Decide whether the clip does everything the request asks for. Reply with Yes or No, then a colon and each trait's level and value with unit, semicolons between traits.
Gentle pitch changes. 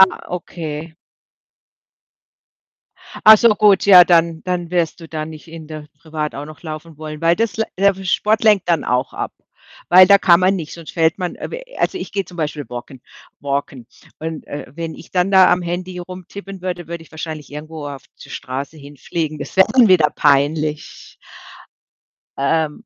No: average, 3.2 semitones